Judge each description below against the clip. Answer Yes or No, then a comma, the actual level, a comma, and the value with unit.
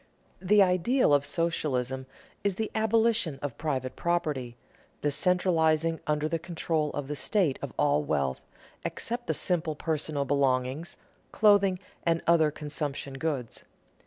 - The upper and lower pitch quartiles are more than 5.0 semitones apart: No, average, 4.2 semitones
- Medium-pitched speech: Yes, medium, 155 Hz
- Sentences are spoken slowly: Yes, slow, 130 wpm